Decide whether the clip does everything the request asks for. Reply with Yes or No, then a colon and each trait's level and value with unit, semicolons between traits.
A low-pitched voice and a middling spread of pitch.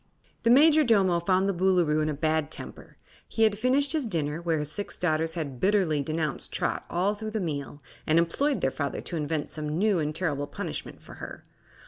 No: medium, 170 Hz; average, 5.0 semitones